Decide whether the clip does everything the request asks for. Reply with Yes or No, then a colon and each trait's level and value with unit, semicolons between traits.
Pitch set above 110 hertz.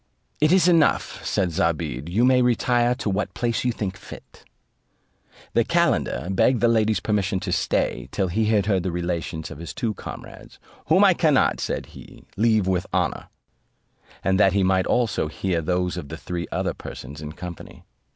No: very low, 95 Hz